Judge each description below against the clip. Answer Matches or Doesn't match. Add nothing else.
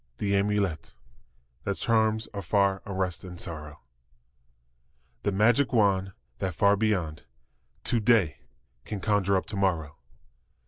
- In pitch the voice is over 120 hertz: Doesn't match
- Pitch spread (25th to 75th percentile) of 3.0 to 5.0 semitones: Doesn't match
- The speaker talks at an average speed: Doesn't match